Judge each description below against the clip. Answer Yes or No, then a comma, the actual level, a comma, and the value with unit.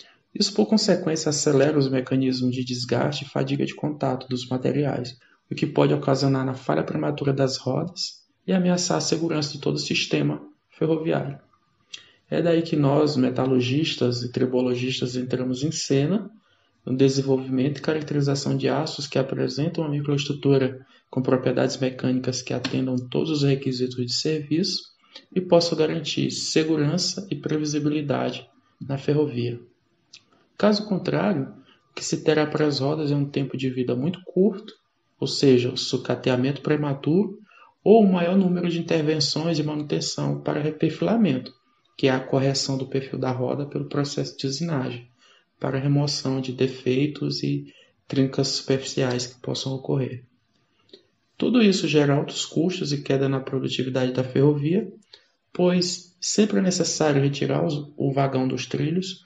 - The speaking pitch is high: No, medium, 140 Hz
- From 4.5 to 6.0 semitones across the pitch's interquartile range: No, average, 3.8 semitones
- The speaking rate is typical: Yes, average, 145 wpm